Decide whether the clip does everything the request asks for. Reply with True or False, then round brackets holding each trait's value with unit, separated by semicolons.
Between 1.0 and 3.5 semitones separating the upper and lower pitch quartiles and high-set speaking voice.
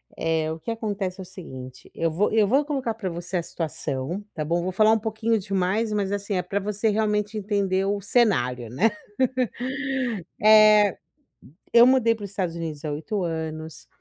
False (4.7 semitones; 195 Hz)